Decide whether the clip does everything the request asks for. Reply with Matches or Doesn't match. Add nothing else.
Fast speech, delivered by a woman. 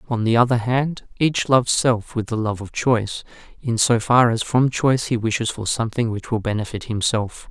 Doesn't match